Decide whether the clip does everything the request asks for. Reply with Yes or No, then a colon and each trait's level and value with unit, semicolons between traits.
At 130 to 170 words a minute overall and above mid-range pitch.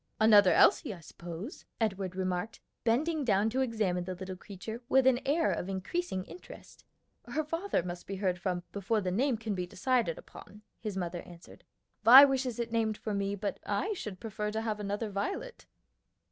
No: average, 180 wpm; high, 210 Hz